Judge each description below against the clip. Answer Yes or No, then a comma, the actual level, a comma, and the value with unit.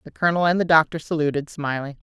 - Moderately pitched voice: Yes, medium, 155 Hz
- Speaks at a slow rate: No, fast, 205 wpm